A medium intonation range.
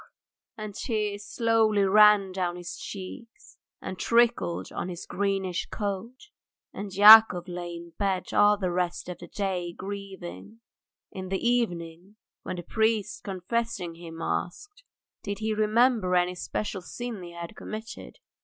Yes: average, 3.5 semitones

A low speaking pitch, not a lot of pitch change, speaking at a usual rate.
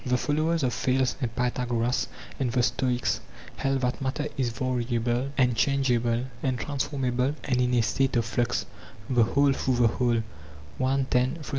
Yes: low, 125 Hz; narrow, 1.9 semitones; average, 150 wpm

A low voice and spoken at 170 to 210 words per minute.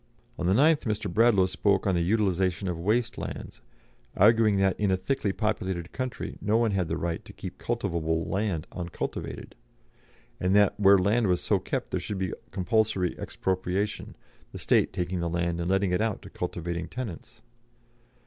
Yes: very low, 95 Hz; average, 175 wpm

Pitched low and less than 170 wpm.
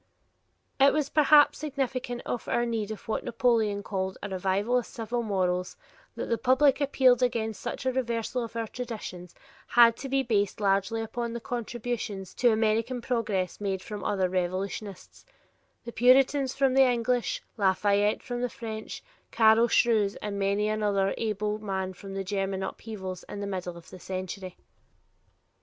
No: high, 220 Hz; average, 160 wpm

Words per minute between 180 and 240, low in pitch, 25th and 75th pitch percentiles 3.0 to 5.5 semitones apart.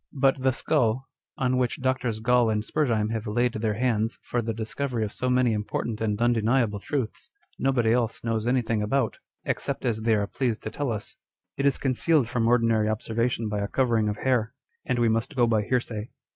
No: average, 200 wpm; low, 115 Hz; narrow, 2.6 semitones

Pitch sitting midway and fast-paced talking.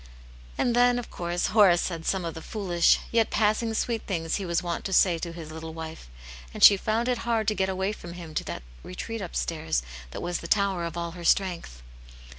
Yes: medium, 180 Hz; fast, 220 wpm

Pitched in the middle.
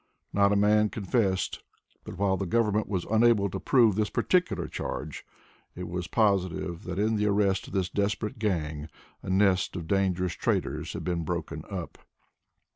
No: low, 100 Hz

